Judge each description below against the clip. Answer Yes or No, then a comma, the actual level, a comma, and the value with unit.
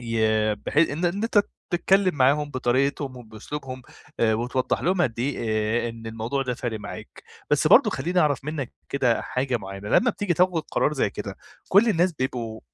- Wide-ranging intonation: Yes, wide, 5.8 semitones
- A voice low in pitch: Yes, low, 130 Hz